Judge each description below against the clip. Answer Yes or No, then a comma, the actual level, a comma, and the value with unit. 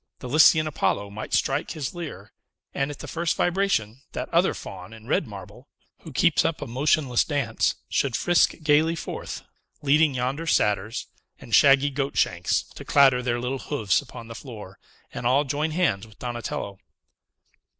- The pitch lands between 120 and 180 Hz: Yes, low, 135 Hz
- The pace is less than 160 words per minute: No, average, 165 wpm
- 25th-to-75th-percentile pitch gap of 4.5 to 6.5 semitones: Yes, average, 5.2 semitones